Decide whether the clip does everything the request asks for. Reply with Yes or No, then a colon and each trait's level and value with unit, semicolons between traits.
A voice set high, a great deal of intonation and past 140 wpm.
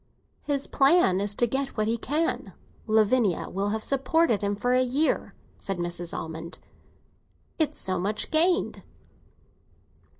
No: high, 225 Hz; wide, 5.9 semitones; slow, 135 wpm